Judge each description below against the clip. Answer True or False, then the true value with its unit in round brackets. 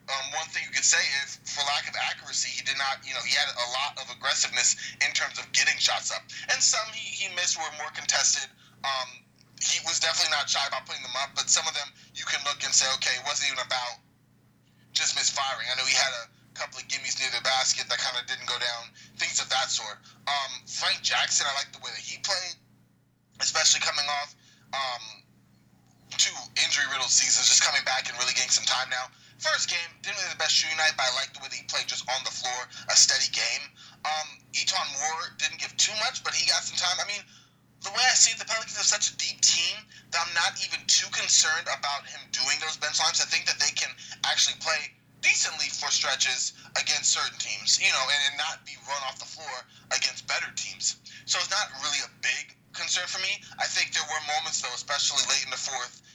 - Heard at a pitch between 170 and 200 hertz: False (135 Hz)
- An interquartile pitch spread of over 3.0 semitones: False (2.7 semitones)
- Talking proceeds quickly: True (230 wpm)